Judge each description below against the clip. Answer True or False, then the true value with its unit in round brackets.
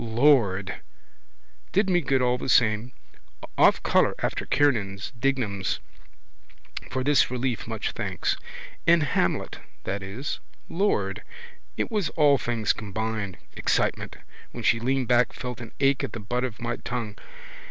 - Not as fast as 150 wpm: True (140 wpm)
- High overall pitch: False (125 Hz)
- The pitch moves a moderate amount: True (4.0 semitones)